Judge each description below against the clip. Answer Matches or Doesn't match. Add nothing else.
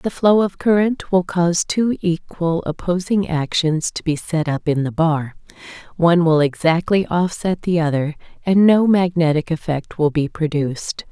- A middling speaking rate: Matches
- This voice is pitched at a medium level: Matches